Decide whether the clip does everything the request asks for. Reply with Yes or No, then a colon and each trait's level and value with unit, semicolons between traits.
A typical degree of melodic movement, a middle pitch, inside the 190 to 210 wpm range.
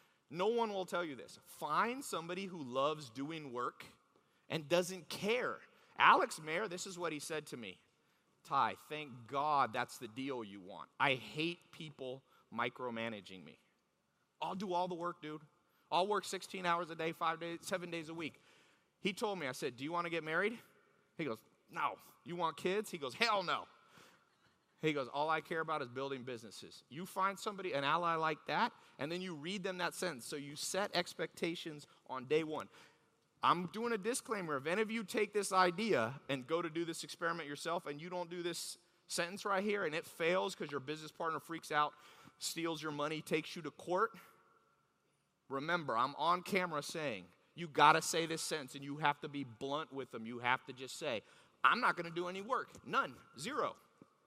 Yes: average, 3.6 semitones; medium, 165 Hz; average, 200 wpm